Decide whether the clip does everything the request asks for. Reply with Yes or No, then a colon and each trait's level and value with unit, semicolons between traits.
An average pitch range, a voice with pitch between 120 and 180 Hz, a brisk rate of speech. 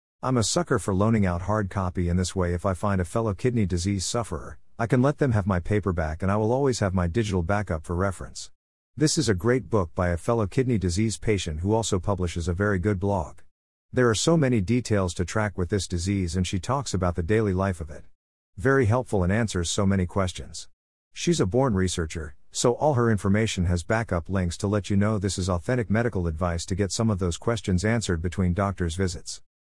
No: average, 4.0 semitones; low, 100 Hz; fast, 220 wpm